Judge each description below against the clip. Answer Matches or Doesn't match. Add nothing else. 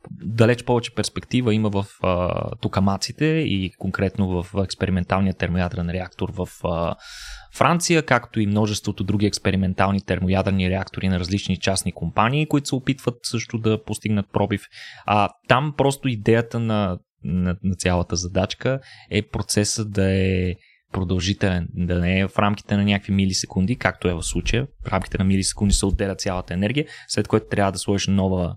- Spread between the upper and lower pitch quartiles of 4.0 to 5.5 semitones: Doesn't match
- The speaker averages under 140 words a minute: Doesn't match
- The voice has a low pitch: Matches